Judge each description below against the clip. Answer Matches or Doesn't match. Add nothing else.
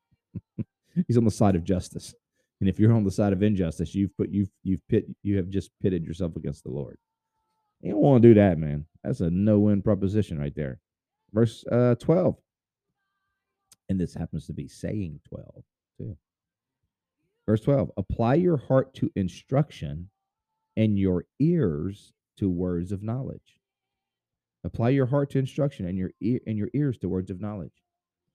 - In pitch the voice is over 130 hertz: Doesn't match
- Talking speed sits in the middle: Matches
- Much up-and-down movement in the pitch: Matches